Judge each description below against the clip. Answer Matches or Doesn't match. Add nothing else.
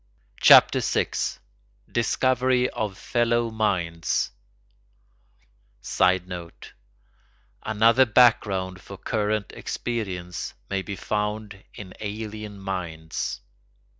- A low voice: Matches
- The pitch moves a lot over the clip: Doesn't match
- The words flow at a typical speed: Doesn't match